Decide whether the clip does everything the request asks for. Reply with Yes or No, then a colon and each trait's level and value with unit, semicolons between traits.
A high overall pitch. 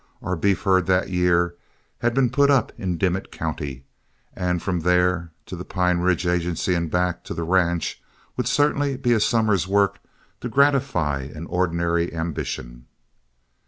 No: very low, 90 Hz